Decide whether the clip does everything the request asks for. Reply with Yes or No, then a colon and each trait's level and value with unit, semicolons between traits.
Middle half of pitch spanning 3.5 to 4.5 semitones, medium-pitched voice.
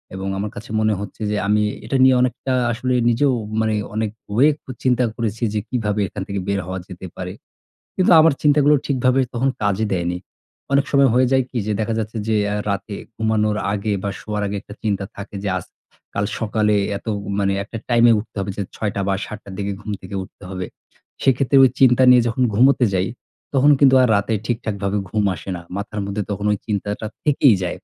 No: average, 3.9 semitones; low, 110 Hz